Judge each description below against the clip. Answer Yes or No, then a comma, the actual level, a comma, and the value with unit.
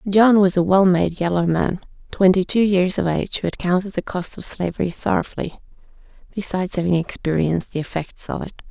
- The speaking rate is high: No, average, 185 wpm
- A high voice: No, medium, 180 Hz